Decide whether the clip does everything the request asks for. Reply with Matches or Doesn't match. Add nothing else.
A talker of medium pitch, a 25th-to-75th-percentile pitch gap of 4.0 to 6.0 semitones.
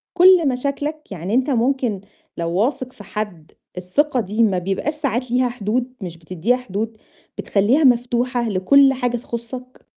Doesn't match